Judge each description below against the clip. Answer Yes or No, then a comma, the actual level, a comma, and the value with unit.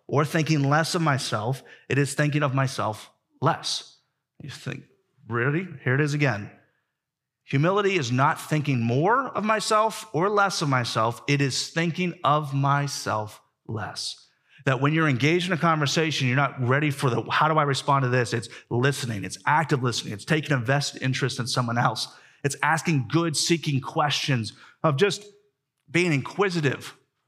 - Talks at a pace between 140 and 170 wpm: Yes, average, 165 wpm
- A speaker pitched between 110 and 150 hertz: Yes, medium, 140 Hz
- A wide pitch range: No, average, 3.6 semitones